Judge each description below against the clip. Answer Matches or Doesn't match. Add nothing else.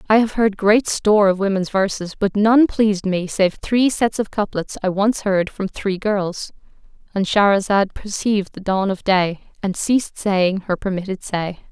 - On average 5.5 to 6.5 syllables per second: Doesn't match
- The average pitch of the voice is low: Doesn't match